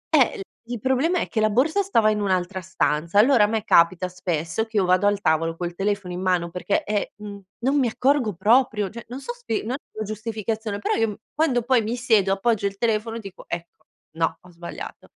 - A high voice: Yes, high, 210 Hz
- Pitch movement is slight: No, average, 4.1 semitones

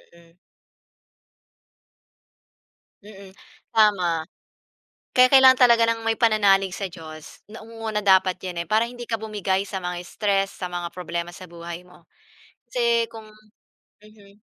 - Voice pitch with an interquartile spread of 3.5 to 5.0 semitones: Yes, average, 4.0 semitones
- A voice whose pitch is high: Yes, high, 200 Hz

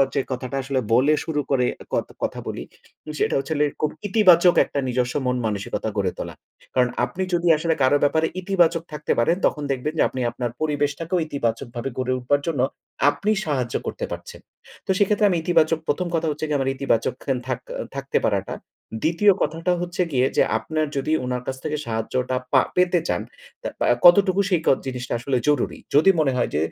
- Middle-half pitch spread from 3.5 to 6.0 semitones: Yes, average, 4.7 semitones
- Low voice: No, medium, 145 Hz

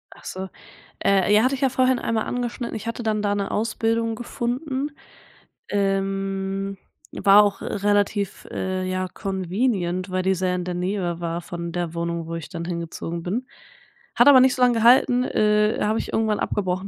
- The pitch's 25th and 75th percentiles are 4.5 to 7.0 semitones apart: No, average, 3.8 semitones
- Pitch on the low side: No, high, 200 Hz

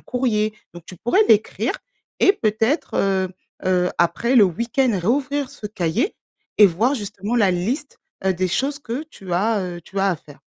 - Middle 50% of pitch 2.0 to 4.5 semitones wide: No, average, 5.2 semitones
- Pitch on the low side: No, high, 215 Hz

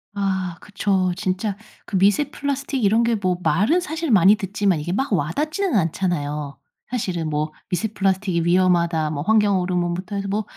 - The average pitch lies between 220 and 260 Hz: No, high, 190 Hz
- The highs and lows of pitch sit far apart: No, average, 3.6 semitones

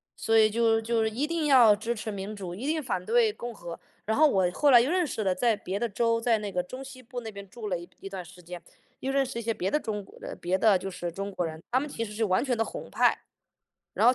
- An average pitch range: Yes, average, 4.0 semitones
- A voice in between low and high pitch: No, high, 220 Hz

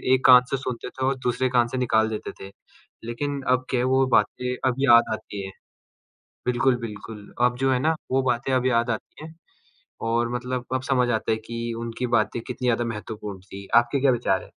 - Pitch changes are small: Yes, narrow, 2.0 semitones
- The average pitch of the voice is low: Yes, low, 120 Hz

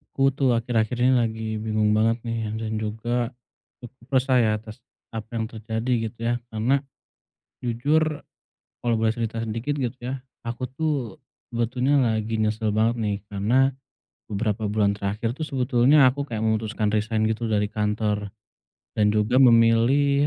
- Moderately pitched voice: No, low, 115 Hz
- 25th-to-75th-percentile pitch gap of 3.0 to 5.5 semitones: No, narrow, 2.6 semitones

